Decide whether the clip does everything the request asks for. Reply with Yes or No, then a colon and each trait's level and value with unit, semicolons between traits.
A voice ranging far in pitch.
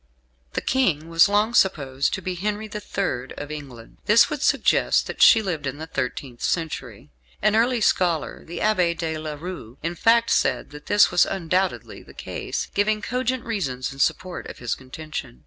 Yes: wide, 6.5 semitones